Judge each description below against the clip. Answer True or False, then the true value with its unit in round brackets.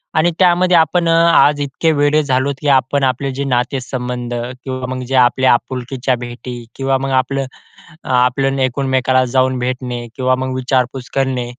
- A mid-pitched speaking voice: False (130 Hz)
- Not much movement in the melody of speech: True (1.5 semitones)